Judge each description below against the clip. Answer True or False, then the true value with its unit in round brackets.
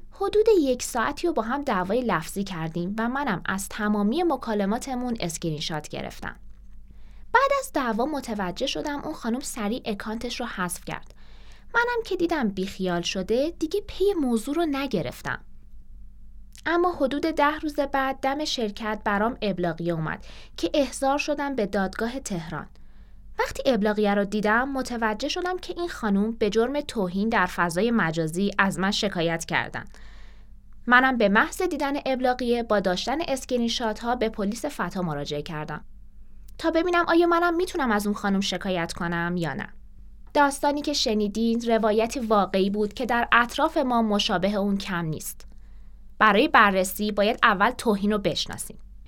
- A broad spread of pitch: True (6.0 semitones)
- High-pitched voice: True (230 Hz)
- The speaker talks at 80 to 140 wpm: False (150 wpm)